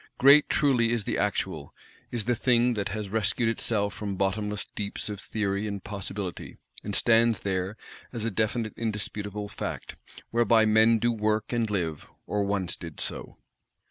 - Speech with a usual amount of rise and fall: No, narrow, 2.3 semitones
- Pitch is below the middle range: Yes, low, 105 Hz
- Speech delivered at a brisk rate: No, average, 160 wpm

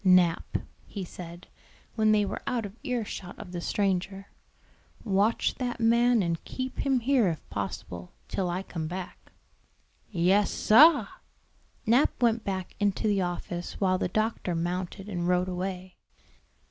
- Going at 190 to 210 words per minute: No, average, 145 wpm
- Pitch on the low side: No, high, 195 Hz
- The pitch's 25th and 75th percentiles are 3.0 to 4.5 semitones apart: Yes, average, 3.9 semitones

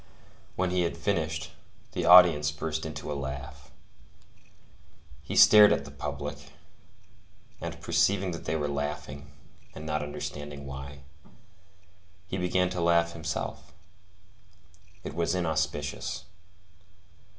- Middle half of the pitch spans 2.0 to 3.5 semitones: Yes, average, 2.9 semitones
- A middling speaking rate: No, slow, 115 wpm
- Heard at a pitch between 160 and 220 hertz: No, very low, 80 Hz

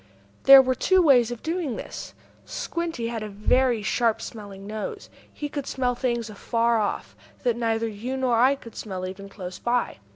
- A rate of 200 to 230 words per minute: No, average, 175 wpm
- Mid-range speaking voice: No, high, 235 Hz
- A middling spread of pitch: Yes, average, 3.5 semitones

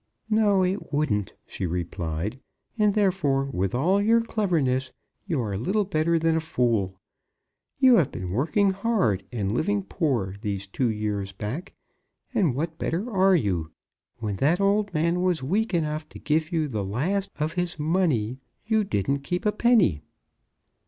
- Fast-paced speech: No, average, 160 wpm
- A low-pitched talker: No, medium, 155 Hz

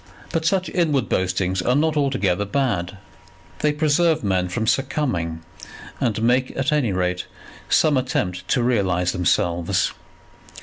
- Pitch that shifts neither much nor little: No, wide, 8.0 semitones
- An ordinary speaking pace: No, slow, 130 wpm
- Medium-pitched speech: No, low, 115 Hz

